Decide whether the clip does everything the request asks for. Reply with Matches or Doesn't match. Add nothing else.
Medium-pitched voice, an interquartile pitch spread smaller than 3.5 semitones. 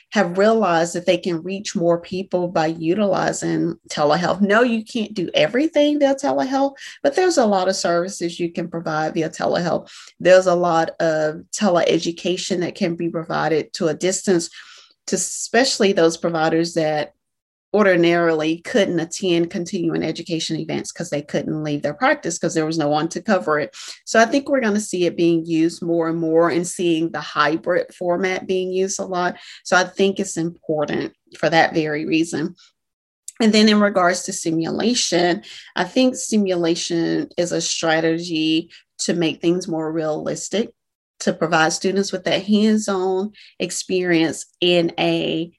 Matches